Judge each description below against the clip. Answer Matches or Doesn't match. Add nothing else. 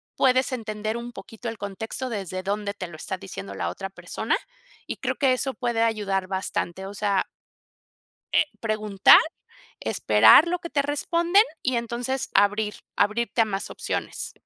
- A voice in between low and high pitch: Doesn't match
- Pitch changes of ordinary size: Matches